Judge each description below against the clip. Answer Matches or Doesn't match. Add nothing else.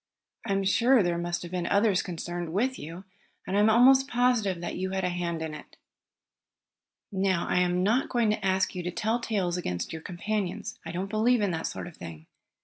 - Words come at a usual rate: Doesn't match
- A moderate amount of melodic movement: Matches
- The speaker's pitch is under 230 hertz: Matches